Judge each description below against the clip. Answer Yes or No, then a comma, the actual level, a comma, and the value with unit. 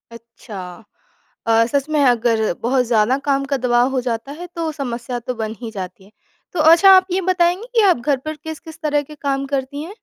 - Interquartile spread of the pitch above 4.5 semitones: Yes, average, 5.0 semitones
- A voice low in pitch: No, very high, 270 Hz